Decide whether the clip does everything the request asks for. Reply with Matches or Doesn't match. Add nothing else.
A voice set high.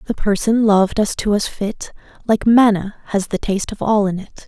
Matches